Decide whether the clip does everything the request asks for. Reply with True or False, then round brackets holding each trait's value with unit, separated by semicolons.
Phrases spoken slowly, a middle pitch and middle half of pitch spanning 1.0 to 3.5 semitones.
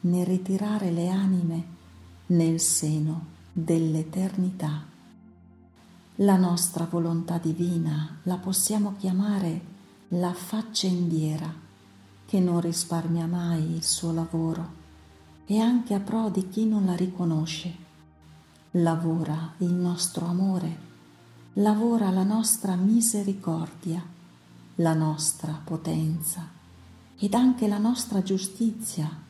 True (100 wpm; 170 Hz; 3.0 semitones)